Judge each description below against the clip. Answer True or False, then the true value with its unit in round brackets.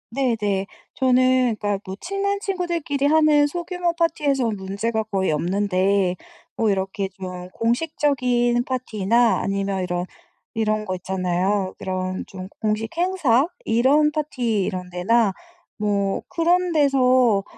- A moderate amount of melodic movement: False (6.5 semitones)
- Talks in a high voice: True (225 Hz)